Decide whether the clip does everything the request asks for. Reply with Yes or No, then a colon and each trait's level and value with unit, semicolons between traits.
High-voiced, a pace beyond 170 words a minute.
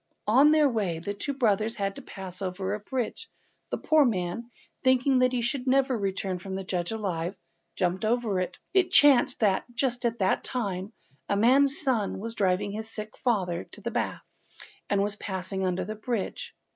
Yes: high, 215 Hz; average, 190 wpm